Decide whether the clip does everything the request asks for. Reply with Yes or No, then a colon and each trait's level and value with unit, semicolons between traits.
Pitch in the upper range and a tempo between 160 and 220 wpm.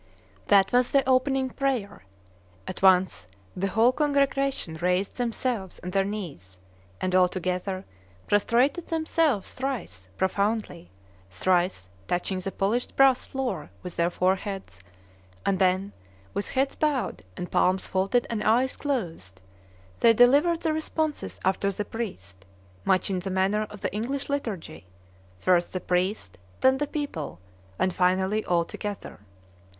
No: high, 200 Hz; slow, 135 wpm